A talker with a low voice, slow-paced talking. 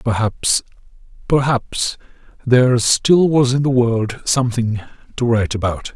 Yes: low, 120 Hz; slow, 120 wpm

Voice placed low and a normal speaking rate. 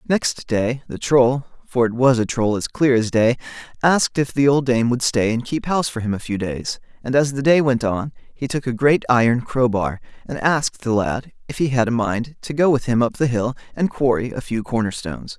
No: low, 125 Hz; fast, 235 wpm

